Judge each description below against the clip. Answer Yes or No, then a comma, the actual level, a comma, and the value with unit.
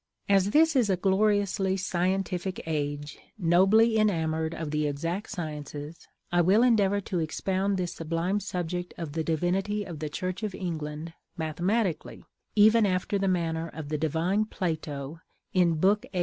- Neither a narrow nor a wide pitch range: Yes, average, 3.7 semitones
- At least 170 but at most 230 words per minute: No, average, 150 wpm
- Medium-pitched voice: Yes, medium, 180 Hz